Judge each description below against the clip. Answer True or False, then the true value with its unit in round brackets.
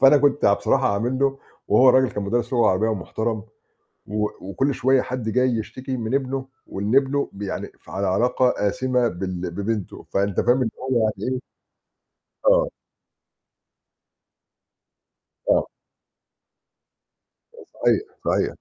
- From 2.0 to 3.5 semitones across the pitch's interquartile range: False (4.2 semitones)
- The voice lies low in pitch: True (120 Hz)